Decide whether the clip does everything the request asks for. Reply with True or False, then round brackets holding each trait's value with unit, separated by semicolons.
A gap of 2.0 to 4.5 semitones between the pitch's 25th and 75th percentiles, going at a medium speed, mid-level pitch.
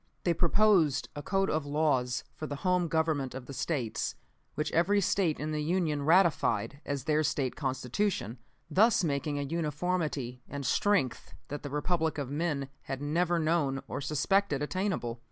True (3.8 semitones; 160 wpm; 150 Hz)